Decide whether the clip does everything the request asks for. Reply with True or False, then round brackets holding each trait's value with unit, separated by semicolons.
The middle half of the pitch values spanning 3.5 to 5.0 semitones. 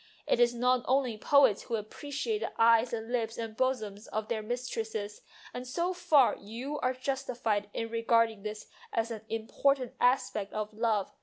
False (2.7 semitones)